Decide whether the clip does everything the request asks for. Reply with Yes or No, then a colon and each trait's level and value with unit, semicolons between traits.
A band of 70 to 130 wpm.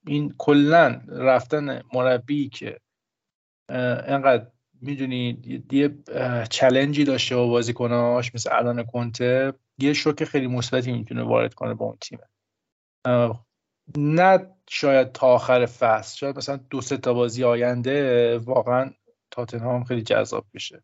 Yes: average, 120 wpm